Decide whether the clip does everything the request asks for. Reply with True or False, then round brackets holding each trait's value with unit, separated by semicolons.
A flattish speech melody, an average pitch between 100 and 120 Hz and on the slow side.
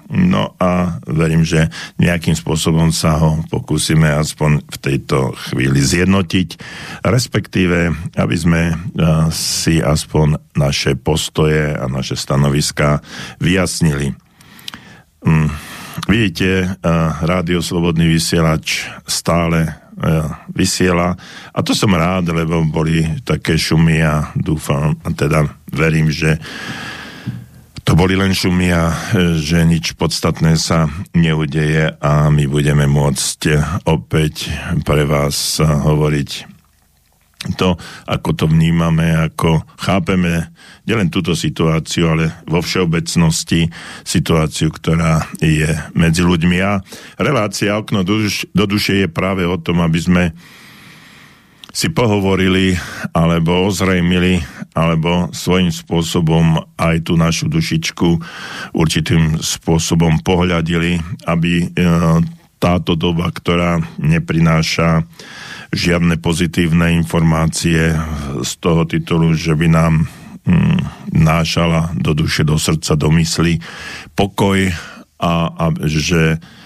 False (1.9 semitones; 85 Hz; 105 wpm)